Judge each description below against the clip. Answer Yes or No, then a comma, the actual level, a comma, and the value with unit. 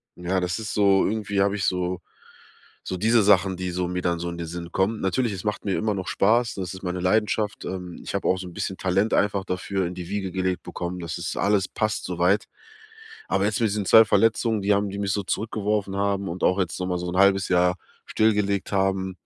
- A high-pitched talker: No, very low, 95 Hz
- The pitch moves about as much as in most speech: No, narrow, 2.2 semitones